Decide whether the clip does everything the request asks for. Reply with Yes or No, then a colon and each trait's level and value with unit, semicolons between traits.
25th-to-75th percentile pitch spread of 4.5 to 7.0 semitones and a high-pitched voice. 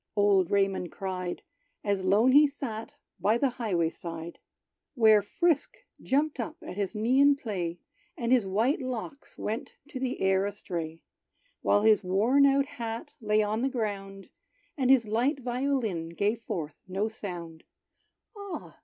Yes: average, 5.1 semitones; high, 215 Hz